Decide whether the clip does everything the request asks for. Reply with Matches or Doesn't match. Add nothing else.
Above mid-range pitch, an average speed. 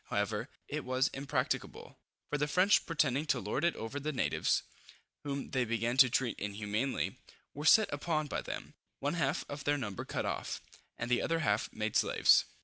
Doesn't match